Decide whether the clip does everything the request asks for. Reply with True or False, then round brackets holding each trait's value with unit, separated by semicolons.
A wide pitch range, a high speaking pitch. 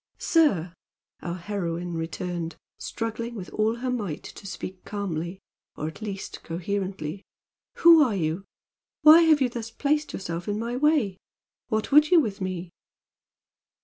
True (5.7 semitones; 200 Hz)